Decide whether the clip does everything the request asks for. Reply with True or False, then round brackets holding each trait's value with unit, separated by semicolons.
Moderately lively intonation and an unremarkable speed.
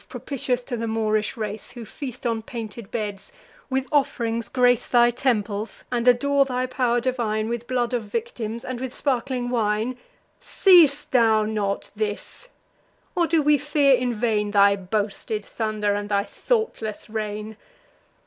True (3.0 semitones; 150 wpm)